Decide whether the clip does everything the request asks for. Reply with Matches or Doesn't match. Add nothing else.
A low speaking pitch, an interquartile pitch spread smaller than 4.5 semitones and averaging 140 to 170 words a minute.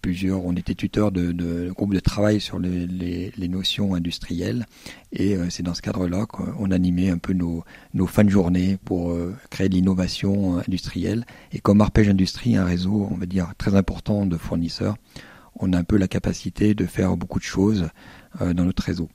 Doesn't match